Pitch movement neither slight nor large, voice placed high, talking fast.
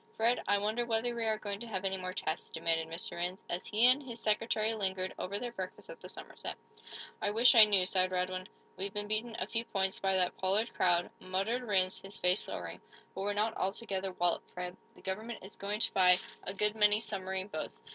Yes: average, 3.0 semitones; high, 200 Hz; fast, 215 wpm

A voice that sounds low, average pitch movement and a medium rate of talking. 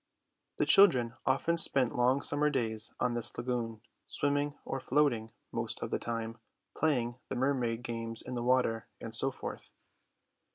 Yes: low, 125 Hz; average, 3.0 semitones; average, 155 wpm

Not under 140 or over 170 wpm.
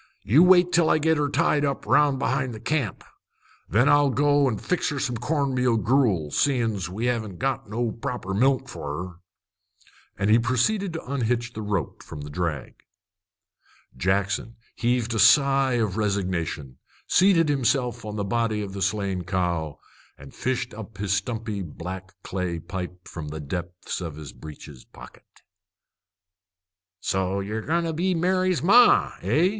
Yes: average, 160 wpm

